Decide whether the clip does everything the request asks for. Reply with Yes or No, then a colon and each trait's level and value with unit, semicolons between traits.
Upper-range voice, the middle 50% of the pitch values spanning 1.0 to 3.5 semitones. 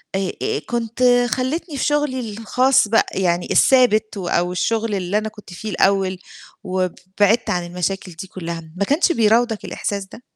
No: high, 205 Hz; average, 4.4 semitones